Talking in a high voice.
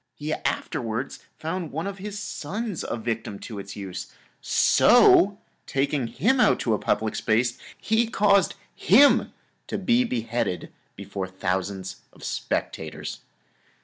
No: low, 125 Hz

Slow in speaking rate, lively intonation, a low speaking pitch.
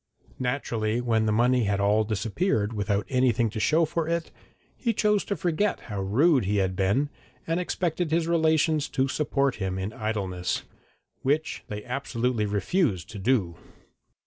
No: average, 155 wpm; wide, 7.2 semitones; low, 120 Hz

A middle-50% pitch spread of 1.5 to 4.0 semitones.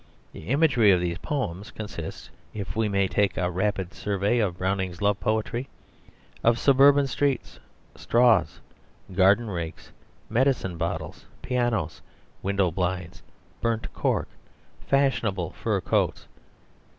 No: average, 4.5 semitones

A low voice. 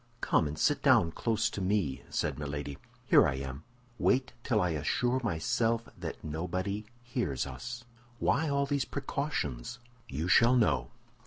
Yes: low, 105 Hz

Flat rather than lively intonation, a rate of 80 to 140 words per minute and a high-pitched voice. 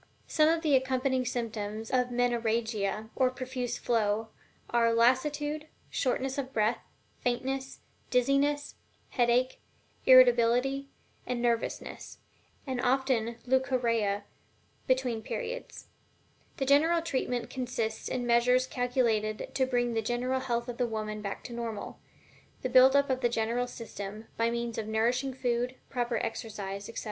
Yes: narrow, 2.2 semitones; slow, 135 wpm; high, 245 Hz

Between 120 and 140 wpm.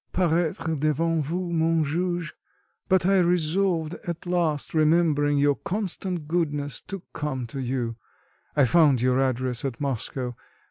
Yes: slow, 135 wpm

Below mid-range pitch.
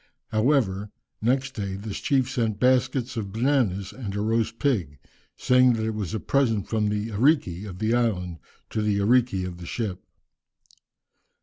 Yes: low, 110 Hz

